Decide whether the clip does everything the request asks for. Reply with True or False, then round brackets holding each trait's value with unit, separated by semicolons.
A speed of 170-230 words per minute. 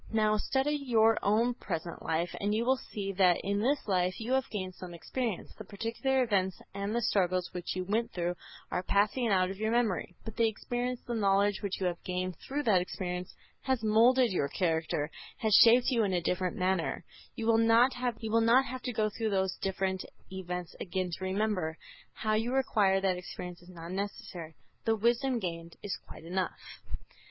True (185 wpm)